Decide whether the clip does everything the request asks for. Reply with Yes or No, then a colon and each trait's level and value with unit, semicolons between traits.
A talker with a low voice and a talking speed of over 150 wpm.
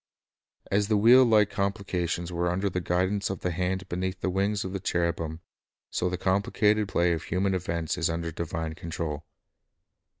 Yes: very low, 90 Hz; average, 175 wpm